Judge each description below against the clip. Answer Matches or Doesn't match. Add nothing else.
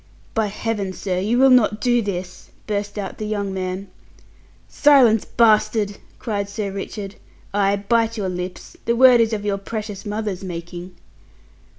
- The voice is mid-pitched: Doesn't match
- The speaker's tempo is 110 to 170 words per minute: Matches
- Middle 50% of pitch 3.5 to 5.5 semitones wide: Doesn't match